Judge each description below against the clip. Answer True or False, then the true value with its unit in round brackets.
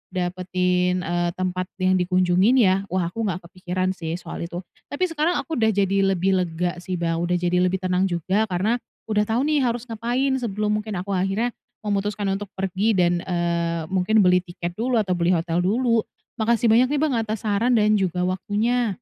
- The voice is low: False (190 Hz)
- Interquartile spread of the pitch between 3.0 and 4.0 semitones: True (3.5 semitones)